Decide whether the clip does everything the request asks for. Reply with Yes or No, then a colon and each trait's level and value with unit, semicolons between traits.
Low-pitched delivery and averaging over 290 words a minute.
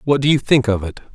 Yes: low, 125 Hz; fast, 315 wpm